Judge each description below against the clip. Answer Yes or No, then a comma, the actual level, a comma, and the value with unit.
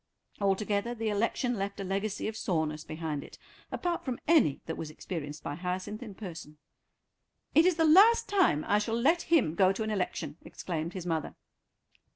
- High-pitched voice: Yes, high, 200 Hz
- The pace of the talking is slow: No, average, 180 wpm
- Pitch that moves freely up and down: Yes, wide, 6.4 semitones